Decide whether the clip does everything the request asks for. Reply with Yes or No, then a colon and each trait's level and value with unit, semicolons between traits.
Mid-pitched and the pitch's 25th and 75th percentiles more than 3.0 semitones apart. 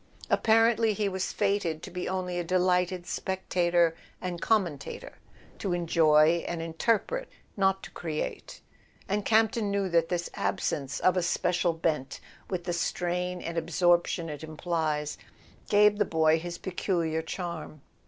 No: medium, 175 Hz; narrow, 2.6 semitones